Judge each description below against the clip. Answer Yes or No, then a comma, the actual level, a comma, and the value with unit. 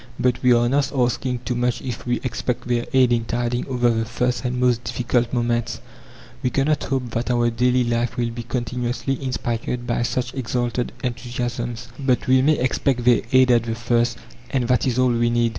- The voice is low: Yes, low, 120 Hz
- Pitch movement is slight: Yes, narrow, 1.1 semitones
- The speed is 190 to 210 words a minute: Yes, average, 195 wpm